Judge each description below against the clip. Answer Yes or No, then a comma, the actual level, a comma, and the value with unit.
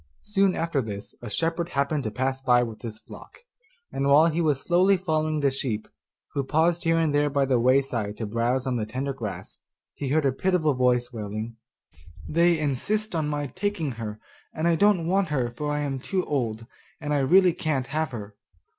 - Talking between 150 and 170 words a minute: No, average, 200 wpm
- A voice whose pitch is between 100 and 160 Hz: Yes, medium, 140 Hz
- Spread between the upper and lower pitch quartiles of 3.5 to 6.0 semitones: Yes, average, 5.1 semitones